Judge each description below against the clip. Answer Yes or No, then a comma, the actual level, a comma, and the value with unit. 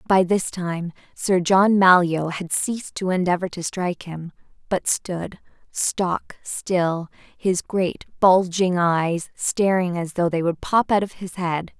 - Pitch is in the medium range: Yes, medium, 180 Hz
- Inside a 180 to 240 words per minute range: No, average, 160 wpm